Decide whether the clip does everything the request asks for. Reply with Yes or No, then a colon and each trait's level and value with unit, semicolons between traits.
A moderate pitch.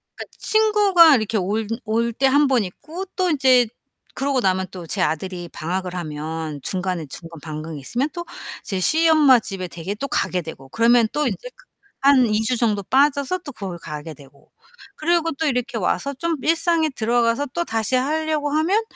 No: high, 235 Hz